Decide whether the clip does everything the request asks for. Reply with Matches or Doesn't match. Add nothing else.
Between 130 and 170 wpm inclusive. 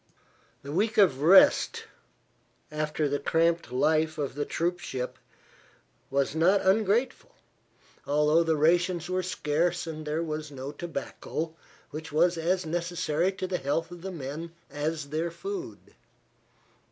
Matches